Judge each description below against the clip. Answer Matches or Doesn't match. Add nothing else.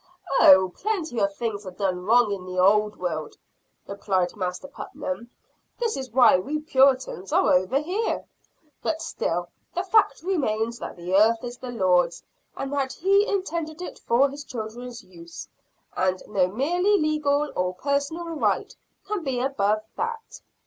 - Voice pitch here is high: Matches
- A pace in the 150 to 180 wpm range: Matches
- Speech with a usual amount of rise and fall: Doesn't match